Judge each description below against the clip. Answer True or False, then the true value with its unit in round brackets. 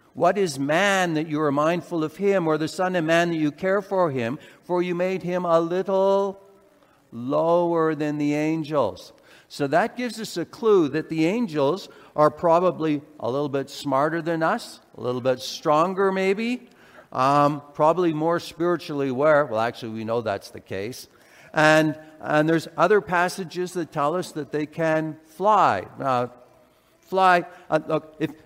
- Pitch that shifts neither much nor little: True (3.3 semitones)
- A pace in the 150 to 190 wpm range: True (170 wpm)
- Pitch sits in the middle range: True (160 Hz)